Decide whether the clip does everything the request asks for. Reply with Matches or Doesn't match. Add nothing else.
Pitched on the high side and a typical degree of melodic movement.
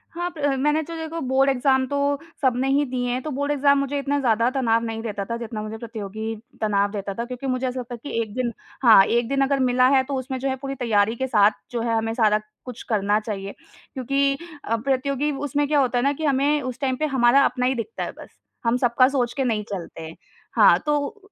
Matches